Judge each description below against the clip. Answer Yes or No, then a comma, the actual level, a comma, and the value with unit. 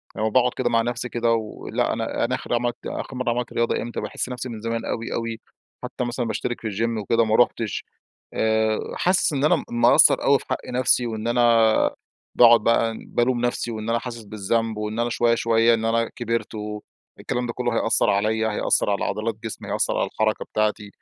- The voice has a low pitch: Yes, low, 115 Hz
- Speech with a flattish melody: Yes, narrow, 1.6 semitones